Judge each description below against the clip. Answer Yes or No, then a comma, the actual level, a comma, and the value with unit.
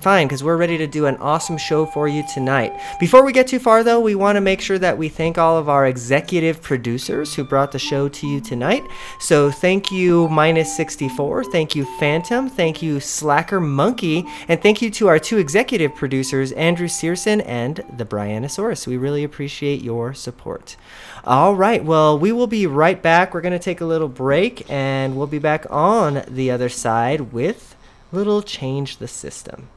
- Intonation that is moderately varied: Yes, average, 4.7 semitones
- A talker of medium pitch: Yes, medium, 155 Hz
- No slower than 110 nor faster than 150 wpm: No, average, 195 wpm